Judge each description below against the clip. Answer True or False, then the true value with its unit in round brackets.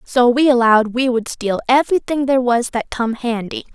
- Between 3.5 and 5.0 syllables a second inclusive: False (5.4 syllables/s)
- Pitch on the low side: False (245 Hz)